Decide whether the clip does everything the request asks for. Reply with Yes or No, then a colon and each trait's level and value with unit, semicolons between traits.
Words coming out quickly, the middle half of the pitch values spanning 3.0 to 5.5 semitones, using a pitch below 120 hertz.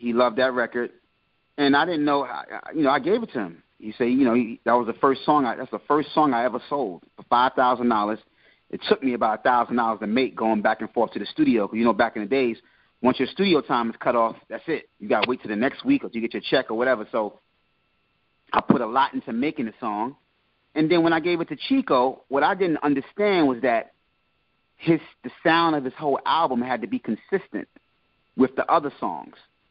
No: fast, 240 wpm; average, 4.9 semitones; low, 130 Hz